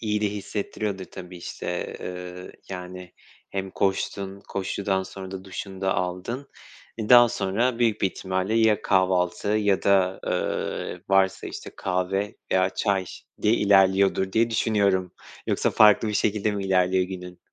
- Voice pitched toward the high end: No, very low, 95 Hz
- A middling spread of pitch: No, narrow, 2.1 semitones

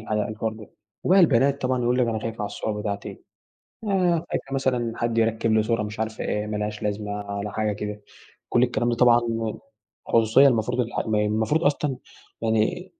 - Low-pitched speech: Yes, low, 115 Hz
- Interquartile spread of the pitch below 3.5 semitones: Yes, average, 2.9 semitones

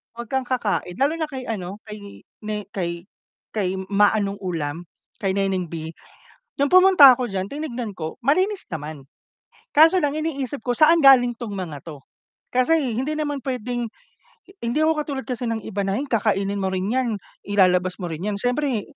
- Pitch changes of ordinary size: No, wide, 6.2 semitones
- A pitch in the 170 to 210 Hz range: No, high, 225 Hz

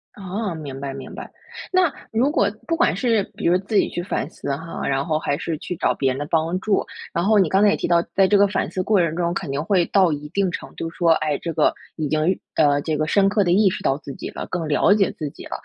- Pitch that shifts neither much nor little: Yes, average, 4.4 semitones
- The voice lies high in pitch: No, medium, 175 Hz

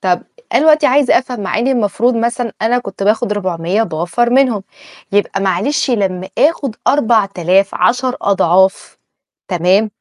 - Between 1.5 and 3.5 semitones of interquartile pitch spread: No, average, 4.6 semitones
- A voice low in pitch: No, high, 210 Hz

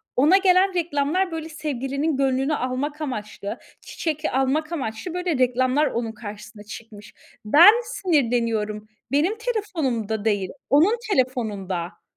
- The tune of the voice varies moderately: No, wide, 6.3 semitones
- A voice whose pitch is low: No, very high, 270 Hz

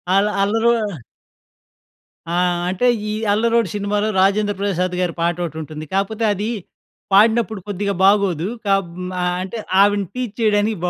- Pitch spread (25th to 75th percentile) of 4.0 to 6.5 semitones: No, narrow, 2.5 semitones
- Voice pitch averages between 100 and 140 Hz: No, high, 200 Hz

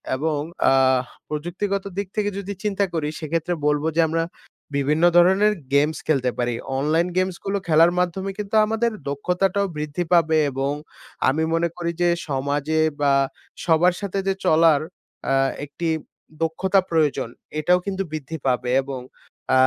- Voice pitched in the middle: Yes, medium, 165 Hz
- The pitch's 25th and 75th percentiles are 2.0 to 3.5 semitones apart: No, average, 4.1 semitones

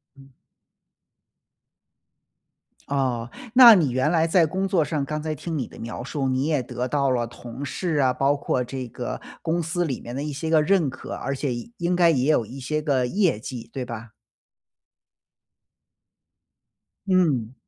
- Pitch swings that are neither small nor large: Yes, average, 4.3 semitones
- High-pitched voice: No, medium, 140 Hz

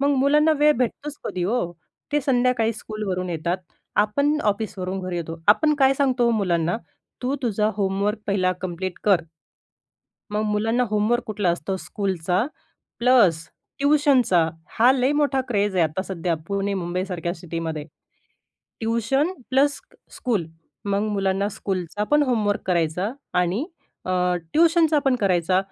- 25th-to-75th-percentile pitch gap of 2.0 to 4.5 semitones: No, wide, 5.6 semitones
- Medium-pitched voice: No, high, 210 Hz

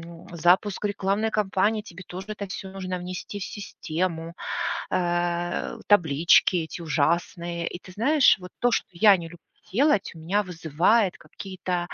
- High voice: No, medium, 180 Hz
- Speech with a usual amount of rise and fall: Yes, average, 3.0 semitones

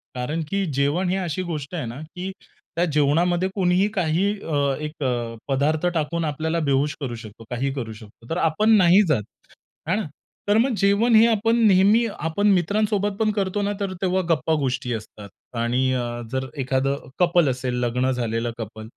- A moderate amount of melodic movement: No, wide, 6.4 semitones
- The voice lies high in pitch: No, medium, 160 Hz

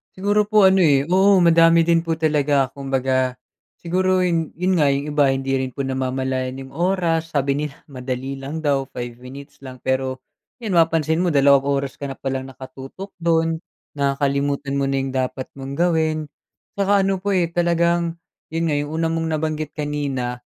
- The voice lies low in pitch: No, medium, 145 Hz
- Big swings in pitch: No, average, 3.8 semitones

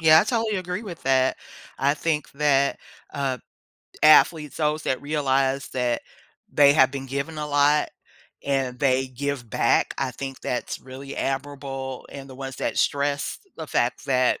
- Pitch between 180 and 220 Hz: No, medium, 140 Hz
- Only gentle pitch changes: Yes, narrow, 2.1 semitones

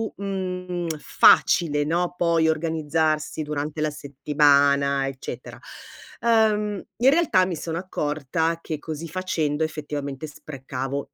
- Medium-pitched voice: Yes, medium, 155 Hz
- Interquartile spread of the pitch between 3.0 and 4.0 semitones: Yes, average, 3.4 semitones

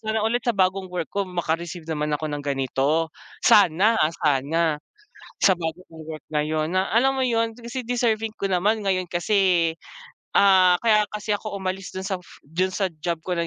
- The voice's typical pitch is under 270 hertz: Yes, medium, 185 Hz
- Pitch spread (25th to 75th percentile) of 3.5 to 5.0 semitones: Yes, average, 4.6 semitones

